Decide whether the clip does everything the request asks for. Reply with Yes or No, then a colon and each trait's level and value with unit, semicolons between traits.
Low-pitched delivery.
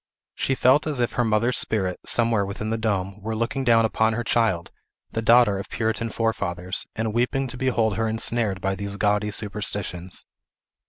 Yes: low, 110 Hz